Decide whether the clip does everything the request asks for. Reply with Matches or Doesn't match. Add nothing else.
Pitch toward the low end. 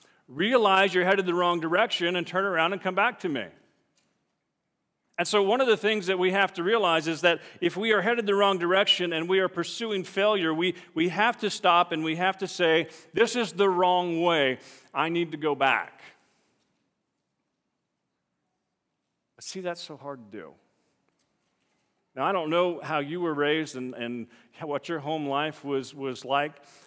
Doesn't match